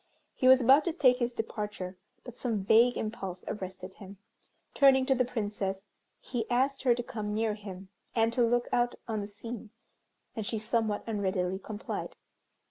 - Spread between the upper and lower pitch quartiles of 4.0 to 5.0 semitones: No, average, 3.2 semitones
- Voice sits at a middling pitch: No, high, 225 Hz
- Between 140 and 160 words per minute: No, average, 170 wpm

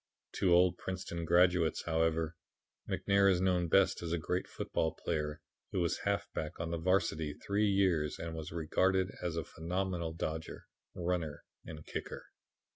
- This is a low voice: Yes, very low, 85 Hz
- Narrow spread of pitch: Yes, narrow, 2.3 semitones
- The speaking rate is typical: Yes, average, 150 wpm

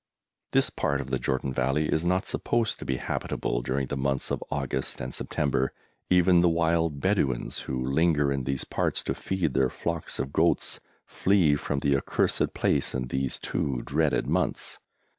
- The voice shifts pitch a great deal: No, average, 3.9 semitones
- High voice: No, very low, 70 Hz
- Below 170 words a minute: No, average, 175 wpm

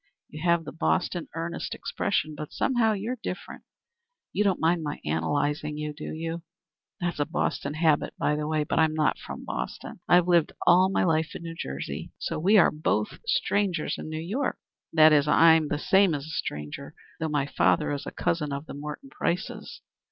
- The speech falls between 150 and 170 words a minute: No, average, 190 wpm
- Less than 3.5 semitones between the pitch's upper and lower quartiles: Yes, average, 2.8 semitones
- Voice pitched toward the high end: No, medium, 160 Hz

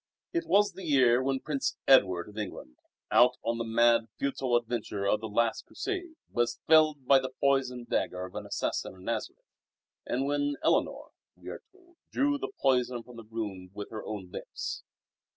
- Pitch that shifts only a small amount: No, average, 4.2 semitones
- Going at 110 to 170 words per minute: No, average, 180 wpm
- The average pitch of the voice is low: Yes, low, 125 Hz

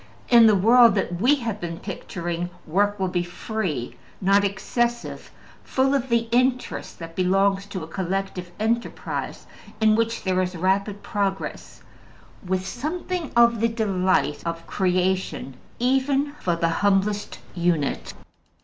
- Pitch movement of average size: Yes, average, 4.3 semitones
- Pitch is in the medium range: No, high, 195 Hz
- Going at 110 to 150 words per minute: Yes, slow, 135 wpm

